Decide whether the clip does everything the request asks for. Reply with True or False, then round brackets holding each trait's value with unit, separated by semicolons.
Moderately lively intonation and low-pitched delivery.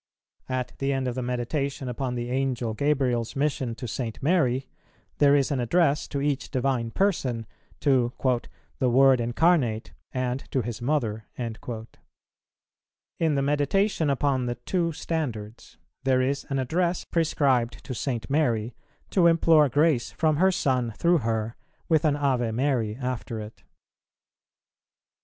True (3.5 semitones; 130 Hz)